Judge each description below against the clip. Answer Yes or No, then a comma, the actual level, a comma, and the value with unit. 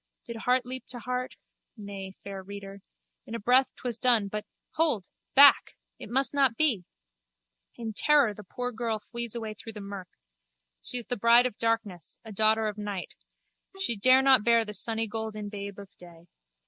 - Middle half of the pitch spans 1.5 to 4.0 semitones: Yes, average, 3.4 semitones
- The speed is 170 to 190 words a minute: Yes, average, 175 wpm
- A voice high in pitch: Yes, high, 225 Hz